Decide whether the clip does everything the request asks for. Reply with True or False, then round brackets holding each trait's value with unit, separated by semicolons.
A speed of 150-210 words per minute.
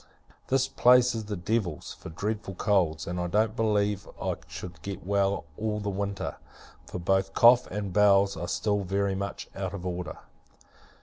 True (170 wpm)